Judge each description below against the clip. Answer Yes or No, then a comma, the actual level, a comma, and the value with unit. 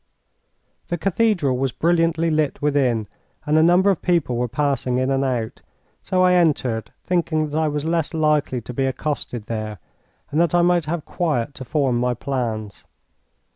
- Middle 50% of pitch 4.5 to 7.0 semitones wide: Yes, average, 5.0 semitones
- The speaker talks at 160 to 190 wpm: Yes, average, 175 wpm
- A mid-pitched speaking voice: Yes, medium, 145 Hz